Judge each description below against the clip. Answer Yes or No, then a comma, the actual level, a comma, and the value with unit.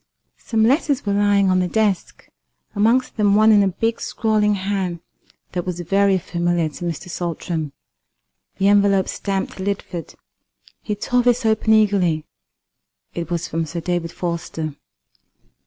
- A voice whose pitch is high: Yes, high, 195 Hz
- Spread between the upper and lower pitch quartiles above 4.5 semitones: No, average, 3.4 semitones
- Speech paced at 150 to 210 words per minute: No, average, 140 wpm